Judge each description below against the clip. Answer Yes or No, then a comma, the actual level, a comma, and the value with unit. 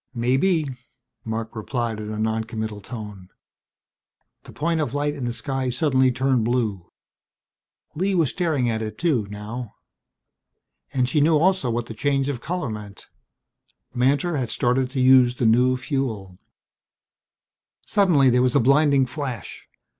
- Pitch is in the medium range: No, low, 125 Hz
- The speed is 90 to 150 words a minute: Yes, average, 145 wpm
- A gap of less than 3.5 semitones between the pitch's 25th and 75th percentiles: No, average, 4.2 semitones